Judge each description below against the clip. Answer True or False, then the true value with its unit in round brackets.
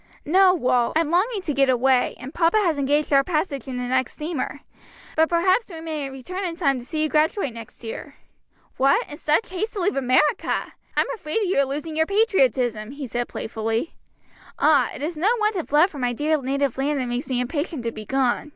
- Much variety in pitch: False (4.7 semitones)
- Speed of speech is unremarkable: False (210 wpm)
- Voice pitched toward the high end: True (290 Hz)